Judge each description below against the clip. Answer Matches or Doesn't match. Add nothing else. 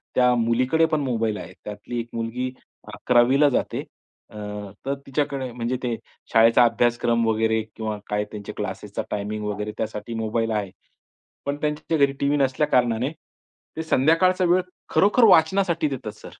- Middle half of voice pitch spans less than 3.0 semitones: Doesn't match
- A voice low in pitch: Matches